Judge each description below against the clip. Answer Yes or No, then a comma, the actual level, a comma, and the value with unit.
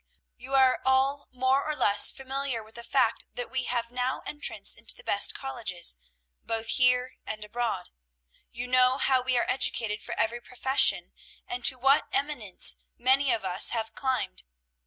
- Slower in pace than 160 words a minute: No, average, 165 wpm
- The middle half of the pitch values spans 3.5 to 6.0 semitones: No, narrow, 2.5 semitones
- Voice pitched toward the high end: Yes, very high, 250 Hz